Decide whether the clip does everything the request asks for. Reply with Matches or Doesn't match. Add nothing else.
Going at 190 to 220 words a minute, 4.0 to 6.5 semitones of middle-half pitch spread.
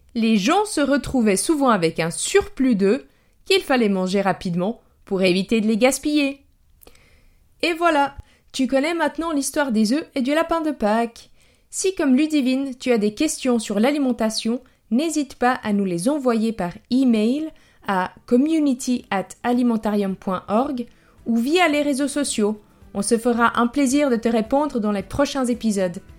Doesn't match